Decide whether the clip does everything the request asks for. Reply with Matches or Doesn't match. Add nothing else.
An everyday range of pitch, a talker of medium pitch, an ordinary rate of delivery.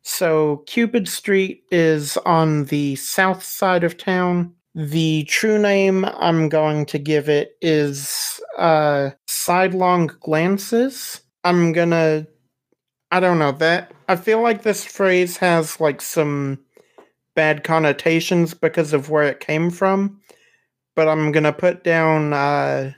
Doesn't match